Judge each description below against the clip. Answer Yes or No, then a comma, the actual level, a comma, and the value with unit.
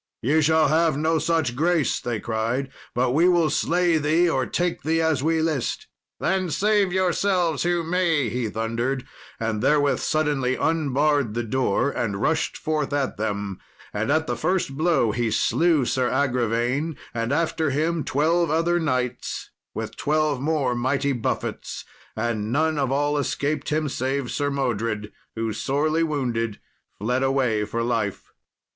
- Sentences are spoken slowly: No, average, 150 wpm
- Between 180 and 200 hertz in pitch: No, medium, 140 Hz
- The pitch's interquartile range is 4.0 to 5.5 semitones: Yes, average, 4.9 semitones